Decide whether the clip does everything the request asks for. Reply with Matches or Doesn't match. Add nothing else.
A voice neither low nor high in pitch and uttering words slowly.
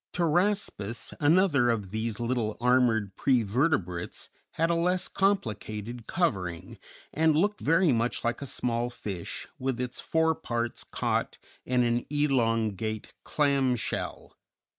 Doesn't match